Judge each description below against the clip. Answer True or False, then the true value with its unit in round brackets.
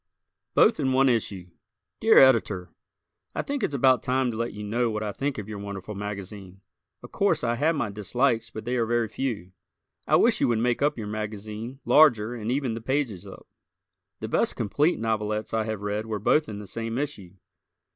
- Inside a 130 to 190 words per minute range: False (200 wpm)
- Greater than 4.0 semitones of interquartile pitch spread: False (3.7 semitones)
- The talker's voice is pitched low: True (110 Hz)